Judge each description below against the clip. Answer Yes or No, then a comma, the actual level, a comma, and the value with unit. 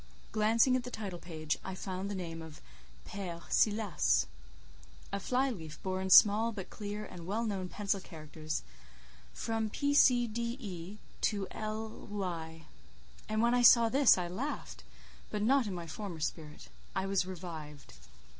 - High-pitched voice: Yes, high, 195 Hz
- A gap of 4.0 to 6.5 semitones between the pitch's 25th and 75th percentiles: Yes, average, 4.5 semitones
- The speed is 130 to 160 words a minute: Yes, average, 155 wpm